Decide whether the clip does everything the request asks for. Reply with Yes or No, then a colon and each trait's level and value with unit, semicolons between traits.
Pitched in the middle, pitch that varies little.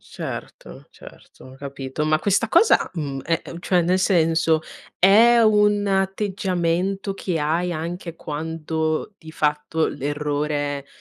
No: medium, 165 Hz; average, 4.2 semitones